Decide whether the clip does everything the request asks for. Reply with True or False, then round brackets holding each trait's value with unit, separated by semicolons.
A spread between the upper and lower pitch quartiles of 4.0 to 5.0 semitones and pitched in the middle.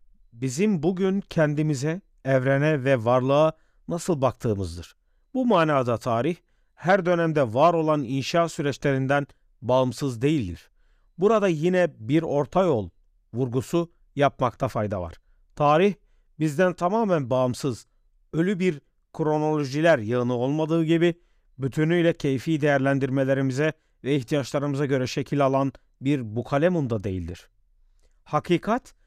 True (4.7 semitones; 145 Hz)